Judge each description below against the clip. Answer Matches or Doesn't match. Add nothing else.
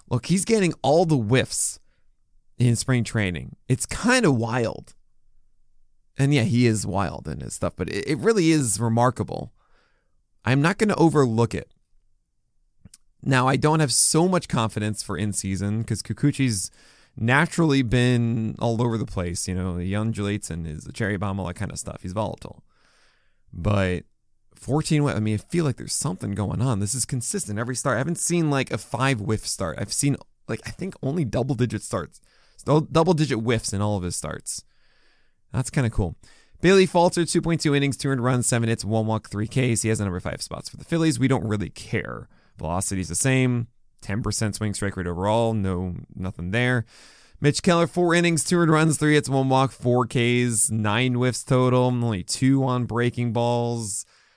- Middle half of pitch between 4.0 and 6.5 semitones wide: Matches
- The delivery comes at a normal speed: Matches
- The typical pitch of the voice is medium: Doesn't match